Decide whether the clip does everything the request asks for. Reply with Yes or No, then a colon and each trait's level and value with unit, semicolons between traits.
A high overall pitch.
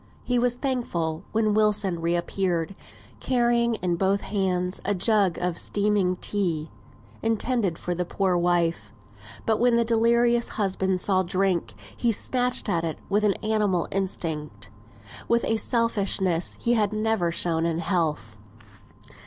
Yes: high, 195 Hz